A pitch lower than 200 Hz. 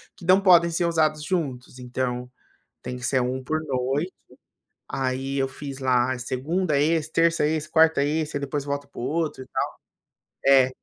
Yes: medium, 140 Hz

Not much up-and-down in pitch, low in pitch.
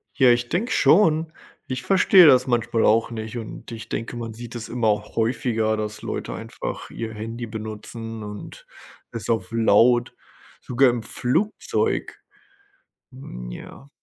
Yes: narrow, 2.3 semitones; low, 115 Hz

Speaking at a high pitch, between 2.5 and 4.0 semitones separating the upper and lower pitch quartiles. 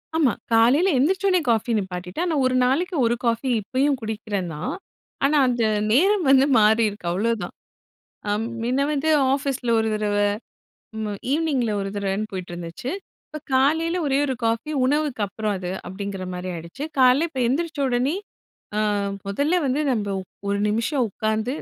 No: high, 240 Hz; wide, 5.6 semitones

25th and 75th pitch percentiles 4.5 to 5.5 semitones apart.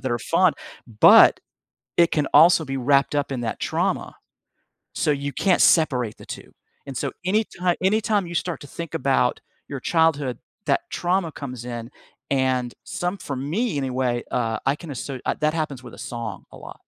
Yes: average, 4.8 semitones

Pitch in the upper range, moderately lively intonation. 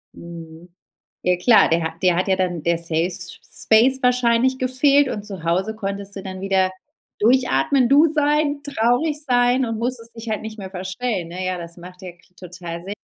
No: high, 200 Hz; wide, 5.8 semitones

